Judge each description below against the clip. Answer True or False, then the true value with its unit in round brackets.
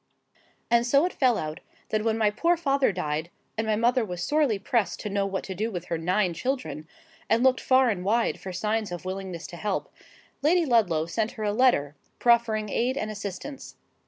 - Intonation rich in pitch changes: False (4.7 semitones)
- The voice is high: True (215 Hz)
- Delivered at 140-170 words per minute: False (200 wpm)